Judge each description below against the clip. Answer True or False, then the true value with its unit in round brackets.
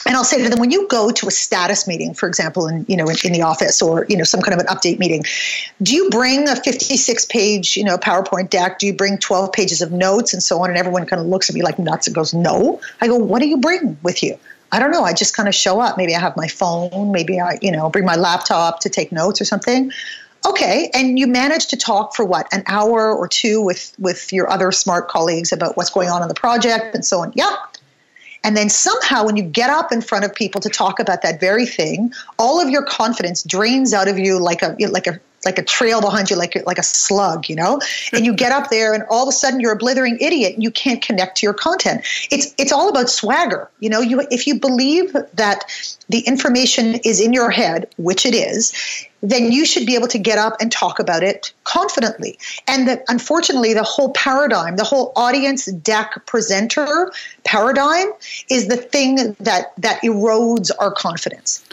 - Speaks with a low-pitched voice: False (220 Hz)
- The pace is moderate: False (235 wpm)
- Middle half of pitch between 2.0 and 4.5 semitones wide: False (5.1 semitones)